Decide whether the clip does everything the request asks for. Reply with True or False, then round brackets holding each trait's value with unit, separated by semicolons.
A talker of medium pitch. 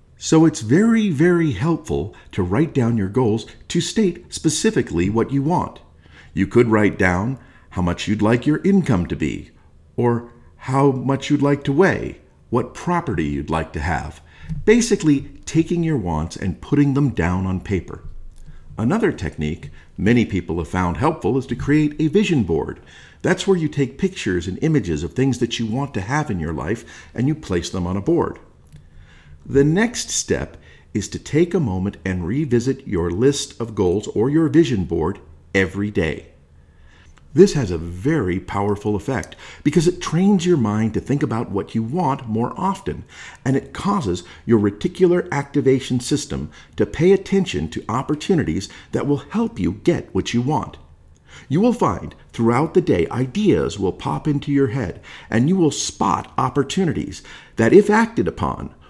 False (115 Hz)